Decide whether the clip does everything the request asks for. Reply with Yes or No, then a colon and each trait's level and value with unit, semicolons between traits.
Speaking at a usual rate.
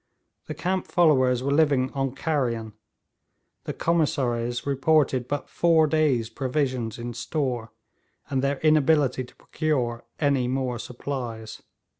No: slow, 120 wpm